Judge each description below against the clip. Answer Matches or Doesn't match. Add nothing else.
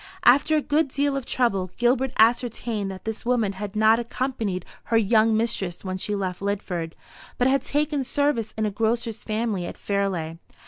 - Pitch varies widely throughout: Doesn't match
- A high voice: Matches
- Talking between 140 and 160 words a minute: Doesn't match